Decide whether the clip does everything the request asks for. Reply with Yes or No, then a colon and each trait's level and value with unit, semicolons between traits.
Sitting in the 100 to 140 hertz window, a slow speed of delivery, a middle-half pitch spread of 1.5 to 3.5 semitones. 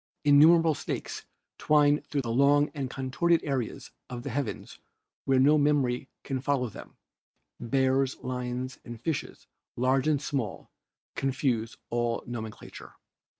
Yes: low, 135 Hz; slow, 120 wpm; average, 2.7 semitones